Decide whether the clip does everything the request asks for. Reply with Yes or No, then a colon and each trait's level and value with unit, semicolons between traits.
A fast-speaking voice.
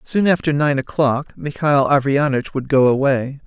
No: average, 155 wpm